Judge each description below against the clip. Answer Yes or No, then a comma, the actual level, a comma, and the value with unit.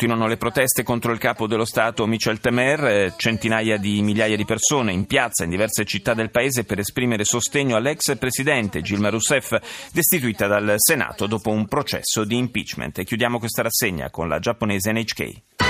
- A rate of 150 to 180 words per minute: Yes, fast, 170 wpm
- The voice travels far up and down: No, narrow, 2.6 semitones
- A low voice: Yes, low, 115 Hz